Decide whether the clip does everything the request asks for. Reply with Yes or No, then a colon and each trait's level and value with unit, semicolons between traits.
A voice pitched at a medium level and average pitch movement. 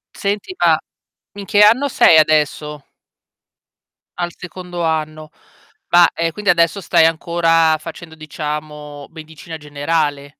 No: medium, 160 Hz; narrow, 2.3 semitones